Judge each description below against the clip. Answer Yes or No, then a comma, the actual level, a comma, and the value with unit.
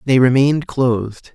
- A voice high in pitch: No, low, 130 Hz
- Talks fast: No, slow, 135 wpm